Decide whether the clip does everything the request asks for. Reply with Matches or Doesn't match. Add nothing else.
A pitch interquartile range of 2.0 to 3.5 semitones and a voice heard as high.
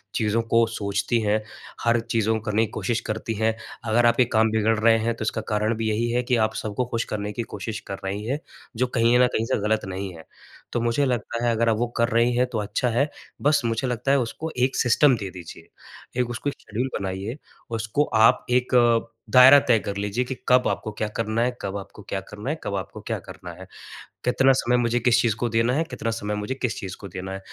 Doesn't match